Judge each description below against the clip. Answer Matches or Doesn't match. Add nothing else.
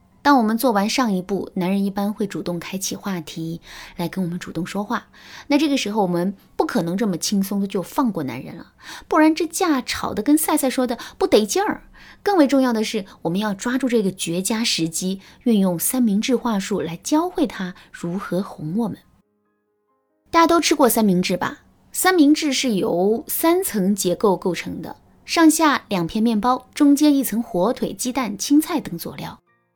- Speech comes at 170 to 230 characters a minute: Doesn't match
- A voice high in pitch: Matches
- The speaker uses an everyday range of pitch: Doesn't match